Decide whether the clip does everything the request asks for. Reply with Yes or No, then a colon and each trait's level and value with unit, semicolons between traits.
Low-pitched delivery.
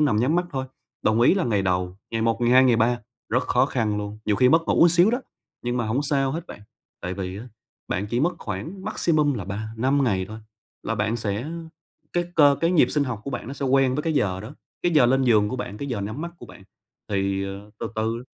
Yes: low, 120 Hz